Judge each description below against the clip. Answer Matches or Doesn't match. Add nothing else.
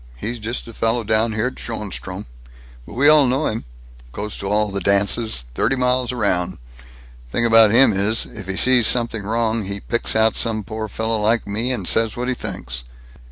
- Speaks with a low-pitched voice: Matches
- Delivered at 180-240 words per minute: Matches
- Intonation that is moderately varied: Doesn't match